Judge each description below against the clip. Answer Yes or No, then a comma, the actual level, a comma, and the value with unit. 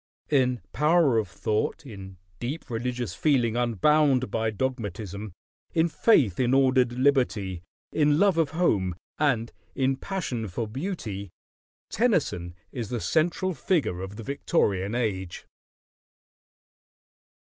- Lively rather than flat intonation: Yes, wide, 6.0 semitones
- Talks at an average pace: No, slow, 115 wpm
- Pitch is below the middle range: Yes, low, 125 Hz